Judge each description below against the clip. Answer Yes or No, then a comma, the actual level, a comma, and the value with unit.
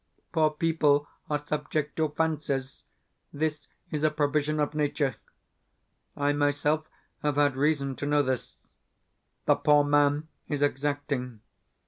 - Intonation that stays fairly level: Yes, narrow, 1.1 semitones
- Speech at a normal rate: No, slow, 125 wpm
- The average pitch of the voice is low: No, medium, 145 Hz